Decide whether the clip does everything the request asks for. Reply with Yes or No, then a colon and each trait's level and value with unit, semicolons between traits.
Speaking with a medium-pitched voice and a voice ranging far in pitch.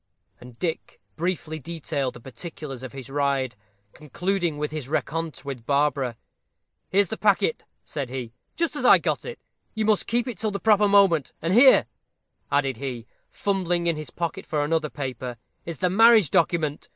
Yes: medium, 155 Hz; wide, 6.0 semitones